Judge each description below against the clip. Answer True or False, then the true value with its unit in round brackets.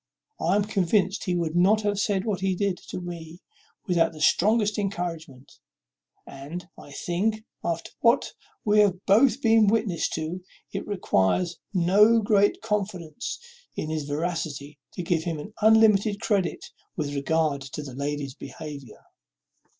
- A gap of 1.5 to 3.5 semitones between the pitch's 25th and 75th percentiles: False (4.7 semitones)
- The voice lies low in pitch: False (180 Hz)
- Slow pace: False (145 wpm)